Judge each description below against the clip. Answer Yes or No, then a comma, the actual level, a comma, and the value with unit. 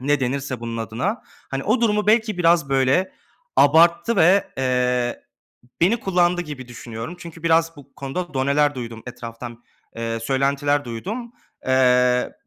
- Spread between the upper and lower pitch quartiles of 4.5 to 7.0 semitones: Yes, wide, 5.6 semitones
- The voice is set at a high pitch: No, medium, 140 Hz